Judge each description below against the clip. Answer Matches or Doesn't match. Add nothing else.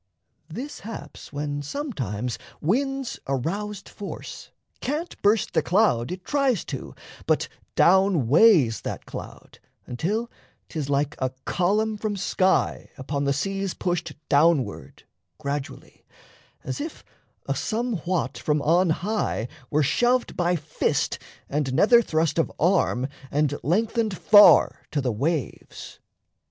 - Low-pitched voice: Doesn't match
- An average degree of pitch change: Doesn't match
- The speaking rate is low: Matches